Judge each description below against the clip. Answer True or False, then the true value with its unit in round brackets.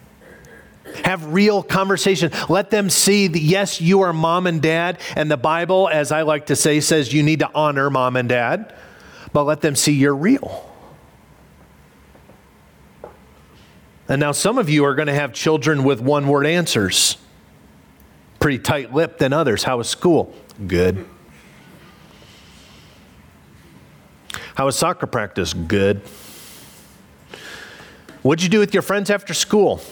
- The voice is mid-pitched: True (150 Hz)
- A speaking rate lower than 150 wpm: True (140 wpm)